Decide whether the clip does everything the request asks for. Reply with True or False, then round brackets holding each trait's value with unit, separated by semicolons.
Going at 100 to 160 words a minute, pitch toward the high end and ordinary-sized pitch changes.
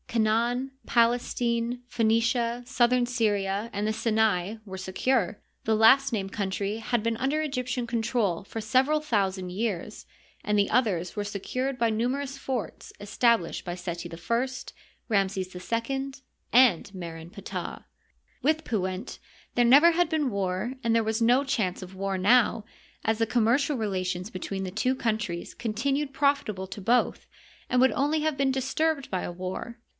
True (155 wpm; 225 Hz; 4.4 semitones)